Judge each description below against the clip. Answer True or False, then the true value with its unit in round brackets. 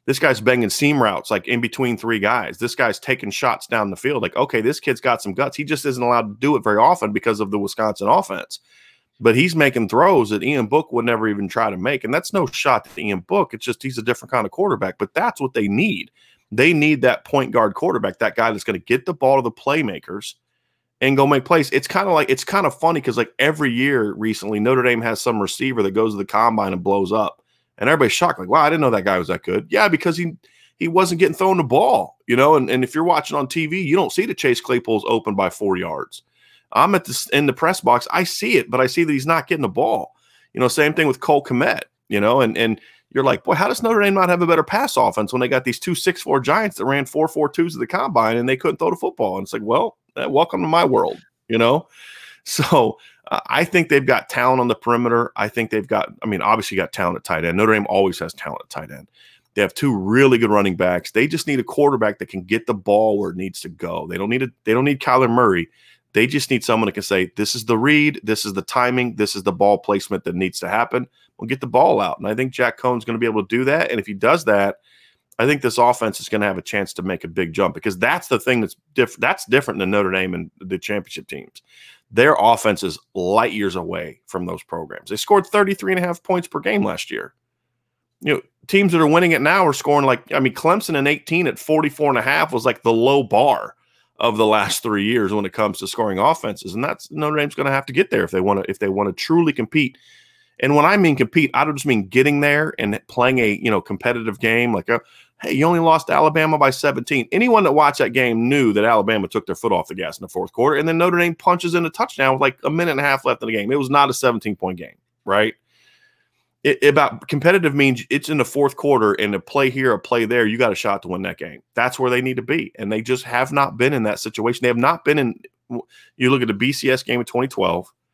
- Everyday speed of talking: False (265 wpm)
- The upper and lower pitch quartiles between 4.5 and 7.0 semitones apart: True (5.1 semitones)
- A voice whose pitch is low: True (125 Hz)